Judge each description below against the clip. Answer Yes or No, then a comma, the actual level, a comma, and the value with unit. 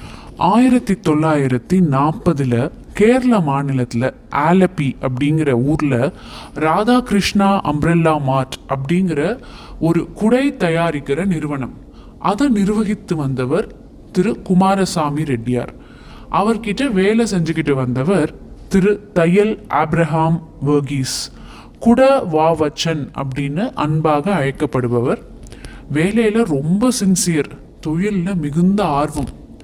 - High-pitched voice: No, medium, 165 Hz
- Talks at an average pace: Yes, average, 85 wpm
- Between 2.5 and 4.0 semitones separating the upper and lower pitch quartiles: No, wide, 5.5 semitones